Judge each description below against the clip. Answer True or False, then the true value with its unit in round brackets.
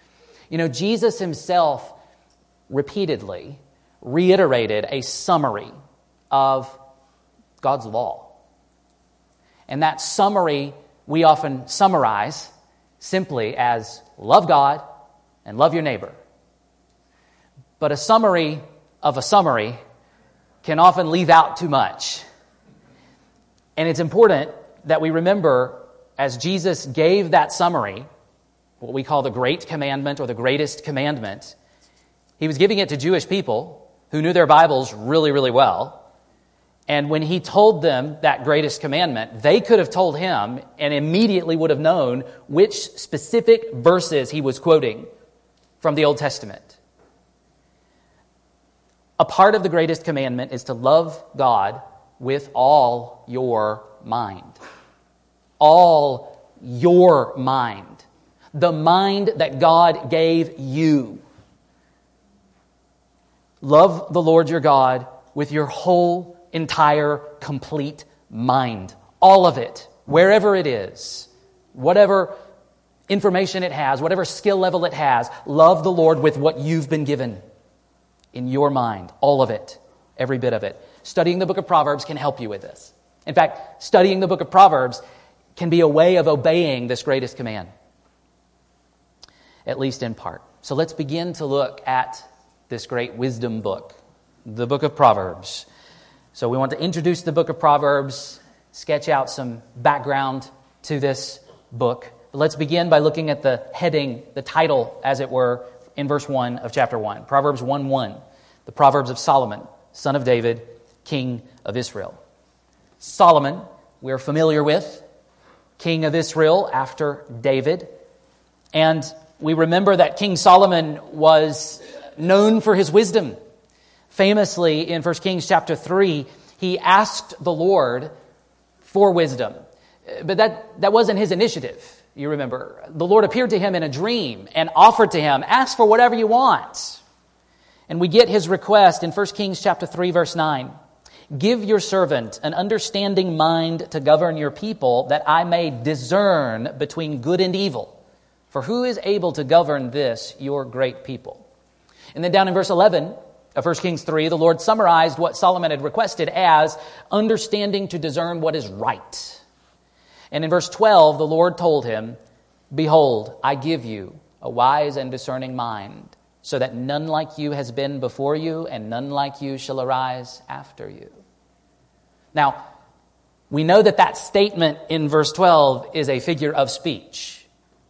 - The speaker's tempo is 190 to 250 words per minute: False (145 wpm)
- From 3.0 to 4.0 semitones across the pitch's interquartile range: False (4.9 semitones)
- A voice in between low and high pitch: True (155 Hz)